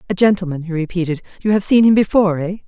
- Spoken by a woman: Yes, female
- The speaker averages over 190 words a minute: Yes, average, 200 wpm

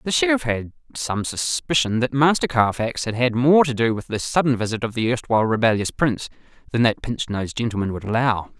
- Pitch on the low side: Yes, low, 120 Hz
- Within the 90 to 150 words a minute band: No, fast, 205 wpm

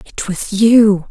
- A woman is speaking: Yes, female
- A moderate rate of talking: Yes, average, 165 wpm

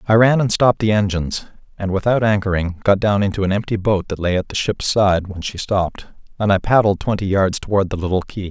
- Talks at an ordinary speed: No, fast, 235 wpm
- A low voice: Yes, low, 100 Hz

